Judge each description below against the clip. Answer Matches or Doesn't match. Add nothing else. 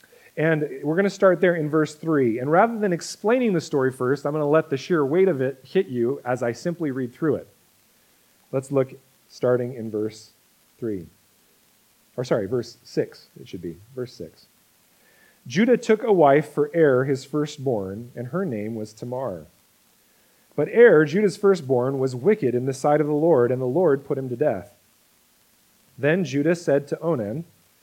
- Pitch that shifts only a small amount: Doesn't match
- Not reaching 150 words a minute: Doesn't match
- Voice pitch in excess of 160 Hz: Doesn't match